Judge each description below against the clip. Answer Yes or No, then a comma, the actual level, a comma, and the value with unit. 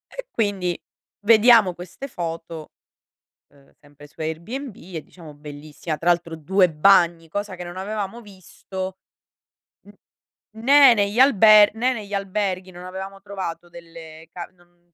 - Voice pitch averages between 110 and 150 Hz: No, medium, 185 Hz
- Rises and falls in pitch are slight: No, average, 3.7 semitones